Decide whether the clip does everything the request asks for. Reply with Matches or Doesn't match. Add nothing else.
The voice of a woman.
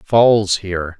Doesn't match